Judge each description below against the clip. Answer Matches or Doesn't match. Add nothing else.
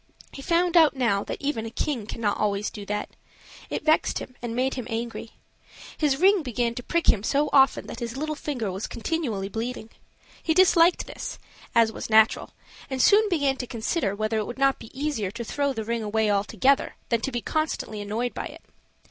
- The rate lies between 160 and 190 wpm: Doesn't match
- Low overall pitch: Doesn't match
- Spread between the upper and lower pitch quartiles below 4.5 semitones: Doesn't match